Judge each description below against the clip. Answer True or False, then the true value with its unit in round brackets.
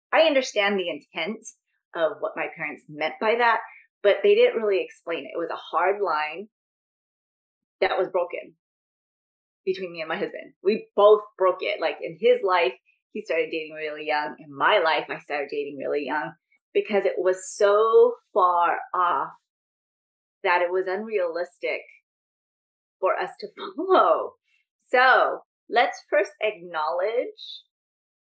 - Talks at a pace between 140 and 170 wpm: True (145 wpm)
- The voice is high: True (210 Hz)